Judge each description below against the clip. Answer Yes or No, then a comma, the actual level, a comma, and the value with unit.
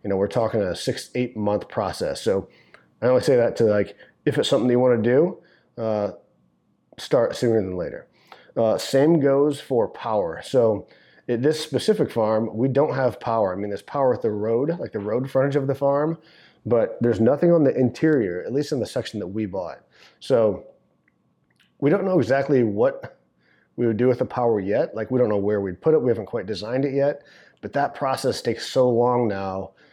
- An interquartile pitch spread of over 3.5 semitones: Yes, average, 4.2 semitones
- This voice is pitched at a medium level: No, low, 125 Hz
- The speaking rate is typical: No, fast, 210 wpm